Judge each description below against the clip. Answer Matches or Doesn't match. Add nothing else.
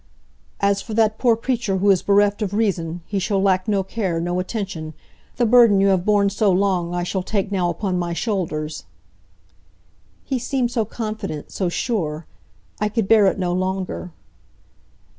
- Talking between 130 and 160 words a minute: Doesn't match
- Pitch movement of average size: Matches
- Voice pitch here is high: Matches